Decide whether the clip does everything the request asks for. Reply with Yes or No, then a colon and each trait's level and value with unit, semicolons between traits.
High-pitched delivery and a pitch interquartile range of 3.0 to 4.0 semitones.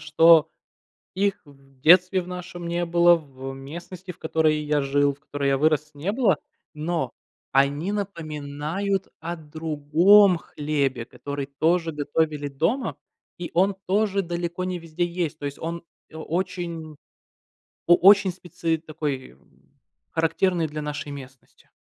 No: medium, 160 Hz; average, 3.4 semitones